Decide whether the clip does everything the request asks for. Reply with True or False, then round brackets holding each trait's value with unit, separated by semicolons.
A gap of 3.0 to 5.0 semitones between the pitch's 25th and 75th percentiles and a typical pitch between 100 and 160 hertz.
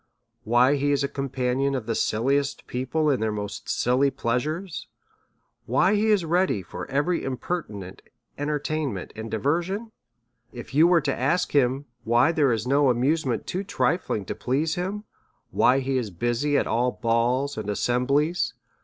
True (4.4 semitones; 135 Hz)